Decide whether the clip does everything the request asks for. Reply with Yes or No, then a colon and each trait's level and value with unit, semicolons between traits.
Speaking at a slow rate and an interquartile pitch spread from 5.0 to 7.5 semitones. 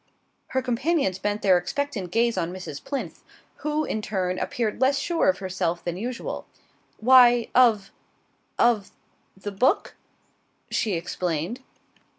Yes: slow, 130 wpm; wide, 5.4 semitones